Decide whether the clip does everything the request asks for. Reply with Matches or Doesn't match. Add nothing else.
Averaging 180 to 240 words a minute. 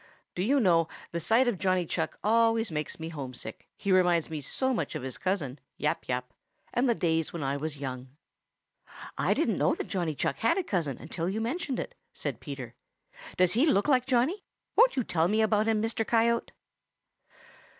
Matches